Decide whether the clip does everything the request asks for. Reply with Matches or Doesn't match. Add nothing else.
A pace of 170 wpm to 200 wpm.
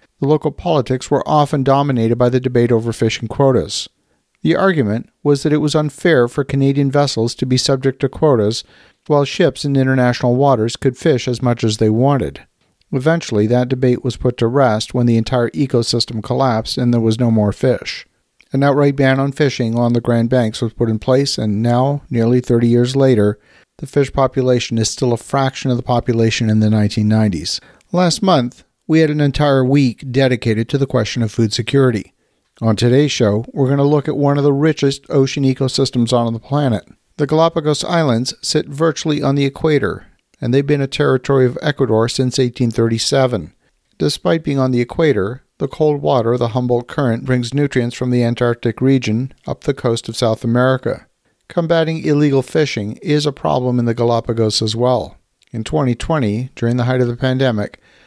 Matches